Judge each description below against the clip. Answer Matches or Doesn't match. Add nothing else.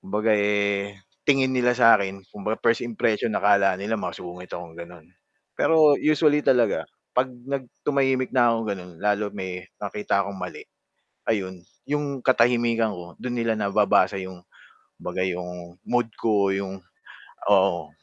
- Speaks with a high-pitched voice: Doesn't match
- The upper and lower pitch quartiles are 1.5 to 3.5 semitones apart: Doesn't match